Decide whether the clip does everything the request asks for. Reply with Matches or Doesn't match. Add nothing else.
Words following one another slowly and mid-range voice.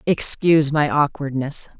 Matches